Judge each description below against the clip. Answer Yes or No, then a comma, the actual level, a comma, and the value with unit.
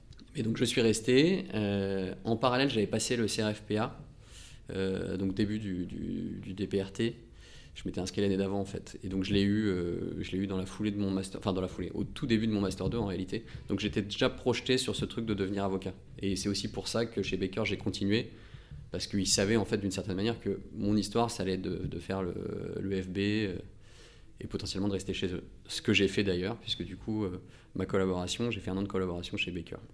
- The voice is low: Yes, low, 100 Hz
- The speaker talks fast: Yes, fast, 240 wpm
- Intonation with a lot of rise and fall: No, average, 2.9 semitones